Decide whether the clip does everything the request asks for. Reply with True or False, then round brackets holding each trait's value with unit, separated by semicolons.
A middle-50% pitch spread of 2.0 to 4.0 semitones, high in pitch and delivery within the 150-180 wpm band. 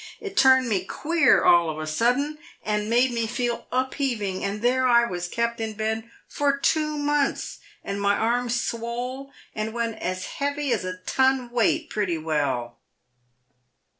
False (4.6 semitones; 235 Hz; 160 wpm)